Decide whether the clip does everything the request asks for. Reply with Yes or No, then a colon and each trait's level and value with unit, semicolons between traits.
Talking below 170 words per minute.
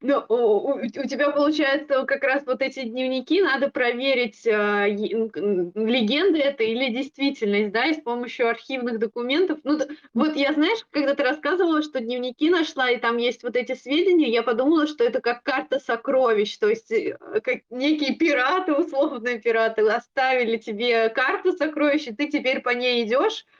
Yes: average, 160 wpm